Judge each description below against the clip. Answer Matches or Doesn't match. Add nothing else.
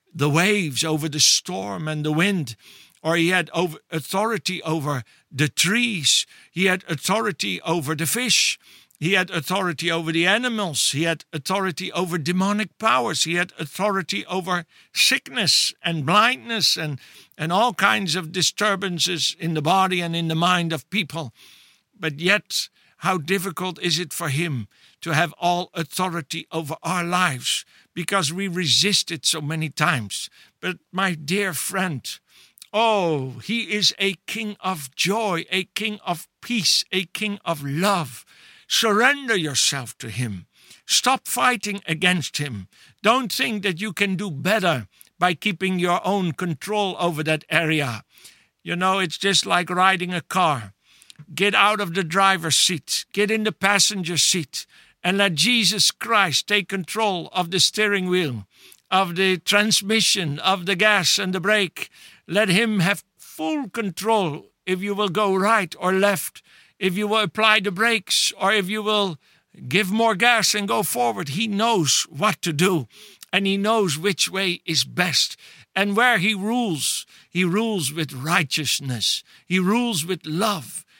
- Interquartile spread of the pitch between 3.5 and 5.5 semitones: Matches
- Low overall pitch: Doesn't match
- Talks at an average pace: Matches